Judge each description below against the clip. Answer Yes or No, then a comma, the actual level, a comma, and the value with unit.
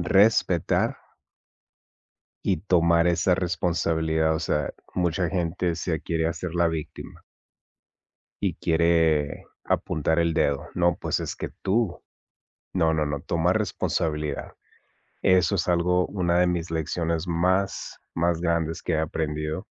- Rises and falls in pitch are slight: Yes, narrow, 1.8 semitones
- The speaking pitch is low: Yes, very low, 85 Hz